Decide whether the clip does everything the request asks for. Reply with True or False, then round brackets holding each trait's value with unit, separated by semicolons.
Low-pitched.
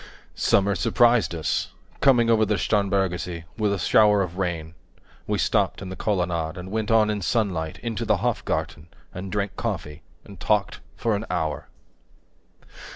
True (100 Hz)